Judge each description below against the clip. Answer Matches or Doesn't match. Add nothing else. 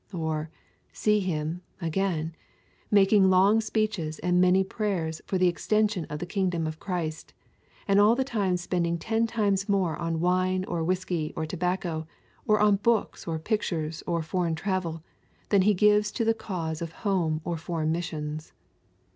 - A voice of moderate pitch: Matches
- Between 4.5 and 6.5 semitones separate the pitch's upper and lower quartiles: Doesn't match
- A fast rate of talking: Doesn't match